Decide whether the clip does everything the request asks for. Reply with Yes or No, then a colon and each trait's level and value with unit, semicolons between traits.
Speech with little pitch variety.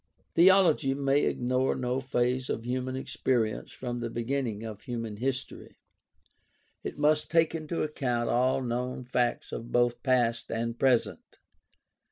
Yes: narrow, 2.1 semitones